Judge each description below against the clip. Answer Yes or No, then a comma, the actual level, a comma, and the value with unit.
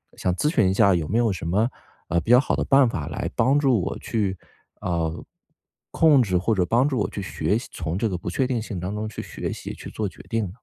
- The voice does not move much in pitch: No, average, 5.0 semitones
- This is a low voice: Yes, low, 105 Hz